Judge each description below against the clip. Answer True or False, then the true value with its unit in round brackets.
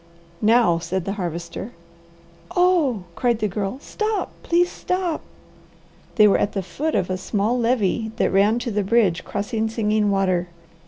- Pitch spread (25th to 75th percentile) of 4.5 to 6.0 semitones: False (4.0 semitones)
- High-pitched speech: True (215 Hz)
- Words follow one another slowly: False (155 wpm)